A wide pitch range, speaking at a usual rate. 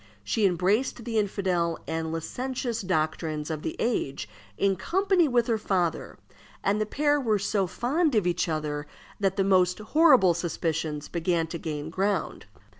Yes: wide, 5.8 semitones; average, 155 wpm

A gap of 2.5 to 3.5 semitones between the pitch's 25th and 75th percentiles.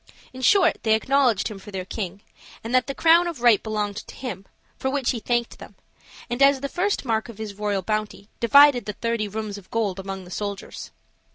No: average, 4.3 semitones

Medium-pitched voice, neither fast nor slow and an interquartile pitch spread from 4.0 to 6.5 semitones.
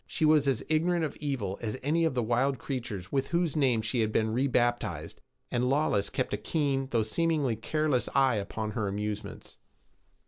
No: low, 130 Hz; average, 180 wpm; average, 5.1 semitones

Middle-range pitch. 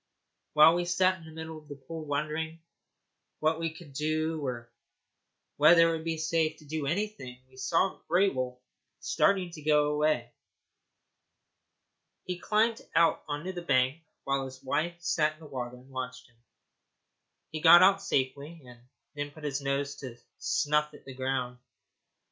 Yes: medium, 155 Hz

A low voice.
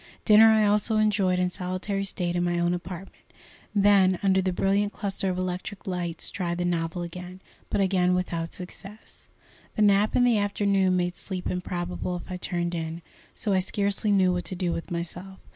No: medium, 185 Hz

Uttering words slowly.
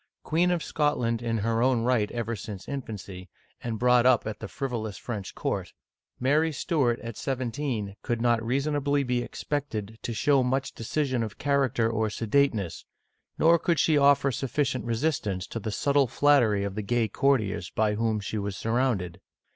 No: average, 165 wpm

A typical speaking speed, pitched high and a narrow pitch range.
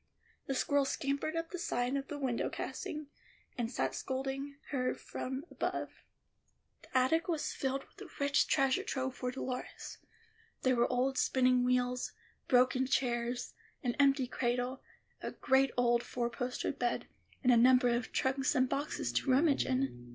Yes: average, 160 wpm; very high, 260 Hz; narrow, 1.6 semitones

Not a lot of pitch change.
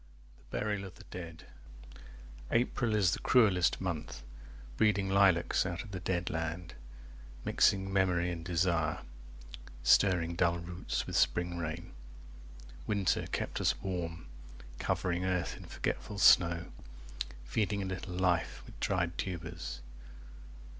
Yes: narrow, 2.2 semitones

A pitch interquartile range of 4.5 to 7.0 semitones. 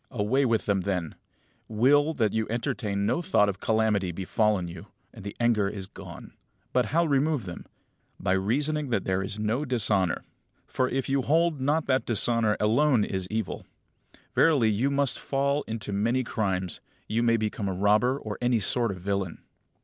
Yes: average, 4.8 semitones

